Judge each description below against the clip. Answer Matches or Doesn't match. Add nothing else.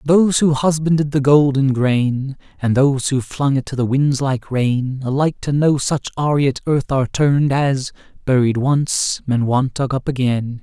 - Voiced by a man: Matches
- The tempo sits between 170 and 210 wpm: Matches